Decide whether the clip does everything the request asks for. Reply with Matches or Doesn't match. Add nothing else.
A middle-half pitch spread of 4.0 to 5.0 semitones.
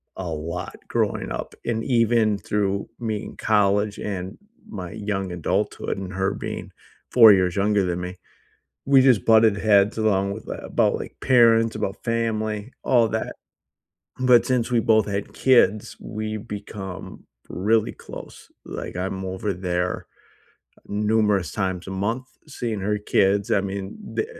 Doesn't match